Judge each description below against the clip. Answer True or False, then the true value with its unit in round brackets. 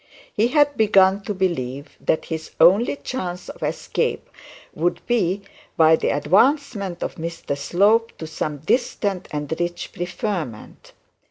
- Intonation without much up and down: False (4.7 semitones)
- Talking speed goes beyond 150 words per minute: False (135 wpm)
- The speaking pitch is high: False (180 Hz)